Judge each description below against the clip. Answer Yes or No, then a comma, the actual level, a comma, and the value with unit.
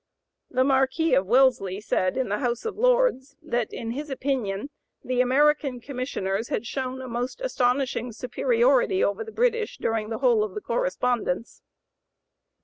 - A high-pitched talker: Yes, very high, 255 Hz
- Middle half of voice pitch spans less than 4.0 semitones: No, average, 4.4 semitones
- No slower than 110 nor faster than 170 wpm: Yes, average, 150 wpm